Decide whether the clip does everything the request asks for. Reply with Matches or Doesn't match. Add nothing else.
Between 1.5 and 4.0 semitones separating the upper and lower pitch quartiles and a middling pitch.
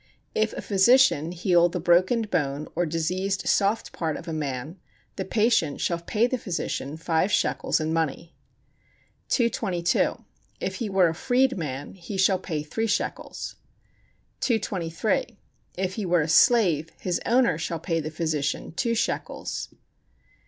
Doesn't match